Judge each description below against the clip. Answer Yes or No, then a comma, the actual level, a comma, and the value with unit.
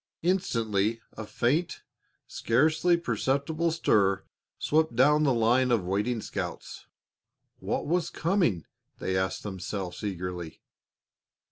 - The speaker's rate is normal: No, slow, 105 wpm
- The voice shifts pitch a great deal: Yes, wide, 8.2 semitones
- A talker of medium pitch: No, low, 120 Hz